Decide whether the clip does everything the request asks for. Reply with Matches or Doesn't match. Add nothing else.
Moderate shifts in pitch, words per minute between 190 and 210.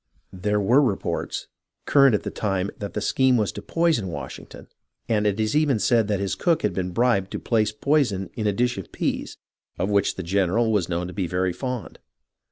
Matches